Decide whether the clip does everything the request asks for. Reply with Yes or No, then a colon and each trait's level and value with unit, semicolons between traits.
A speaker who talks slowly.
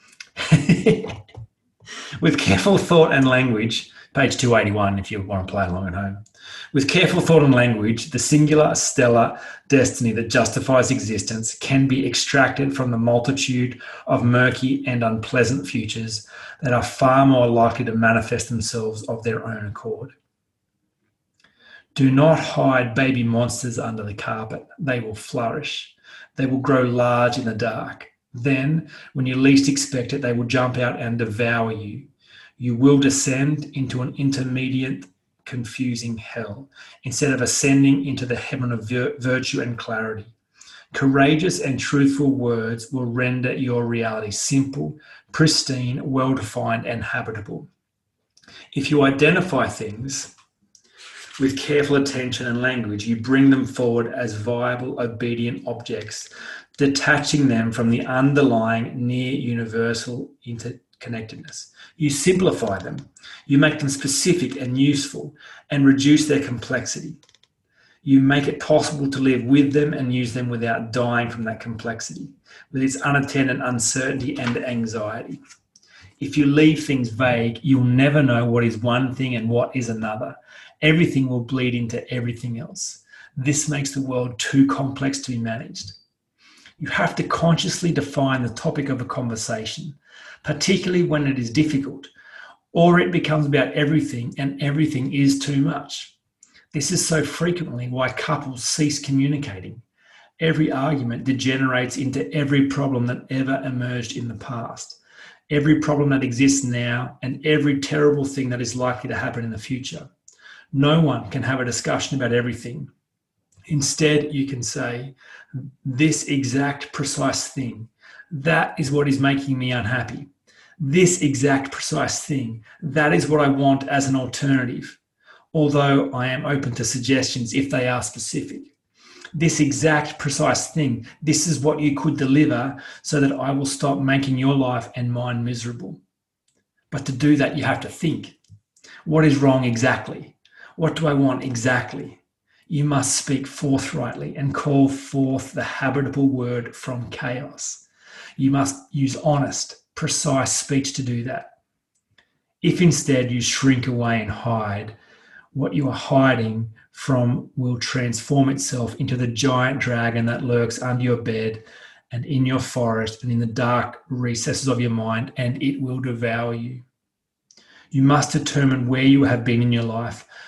No: average, 150 wpm